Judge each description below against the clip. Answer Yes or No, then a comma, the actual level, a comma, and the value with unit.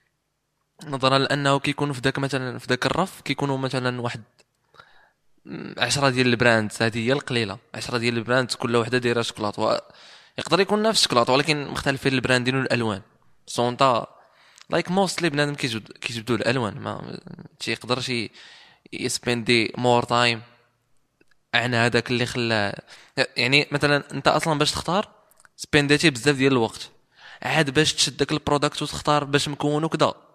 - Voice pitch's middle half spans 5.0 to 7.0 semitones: No, average, 3.5 semitones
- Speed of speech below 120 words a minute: No, fast, 135 wpm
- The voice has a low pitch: Yes, low, 130 Hz